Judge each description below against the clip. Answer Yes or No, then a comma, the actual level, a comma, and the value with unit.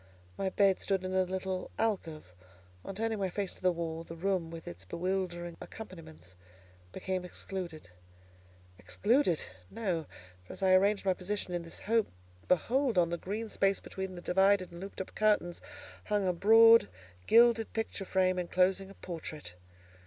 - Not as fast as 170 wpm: Yes, average, 160 wpm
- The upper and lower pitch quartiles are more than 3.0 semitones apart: No, average, 2.7 semitones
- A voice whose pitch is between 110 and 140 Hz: No, medium, 185 Hz